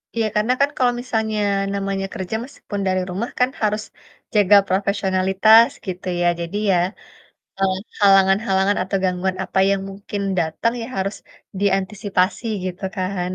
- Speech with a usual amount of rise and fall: No, narrow, 2.2 semitones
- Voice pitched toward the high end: Yes, high, 195 Hz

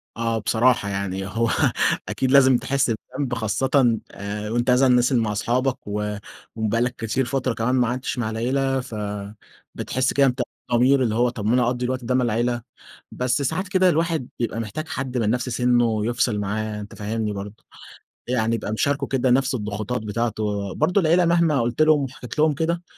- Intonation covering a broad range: No, average, 3.4 semitones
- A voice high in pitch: No, low, 120 Hz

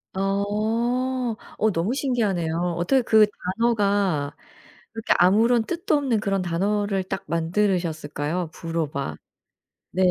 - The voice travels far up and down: No, average, 4.9 semitones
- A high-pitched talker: Yes, high, 200 Hz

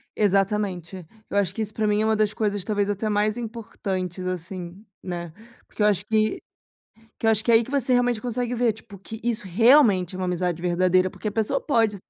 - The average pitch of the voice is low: No, high, 210 Hz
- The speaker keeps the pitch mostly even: No, average, 3.2 semitones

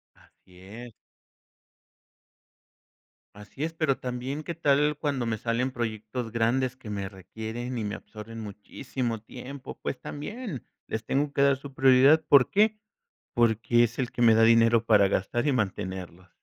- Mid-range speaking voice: No, low, 120 Hz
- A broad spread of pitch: No, average, 3.9 semitones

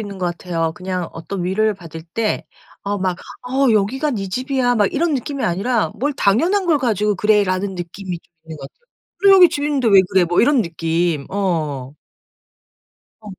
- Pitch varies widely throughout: Yes, wide, 6.4 semitones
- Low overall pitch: No, high, 200 Hz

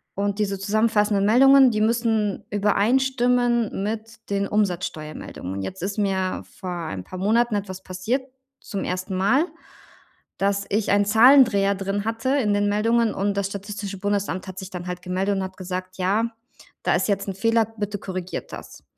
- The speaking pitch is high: Yes, high, 205 Hz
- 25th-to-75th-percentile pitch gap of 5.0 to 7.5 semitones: No, average, 2.9 semitones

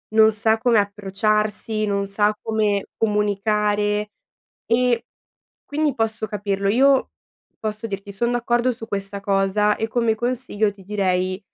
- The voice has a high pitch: Yes, high, 210 Hz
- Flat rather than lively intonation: Yes, narrow, 1.9 semitones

